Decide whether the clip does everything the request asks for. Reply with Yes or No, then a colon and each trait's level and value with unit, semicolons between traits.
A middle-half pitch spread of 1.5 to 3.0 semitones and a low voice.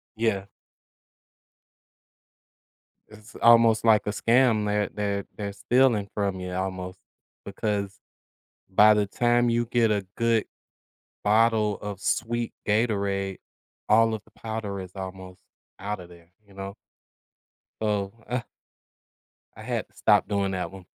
Yes: narrow, 2.5 semitones; low, 105 Hz